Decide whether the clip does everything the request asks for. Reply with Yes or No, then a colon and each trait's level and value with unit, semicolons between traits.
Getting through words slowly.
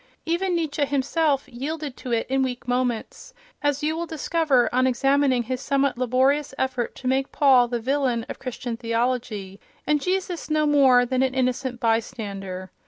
No: average, 165 wpm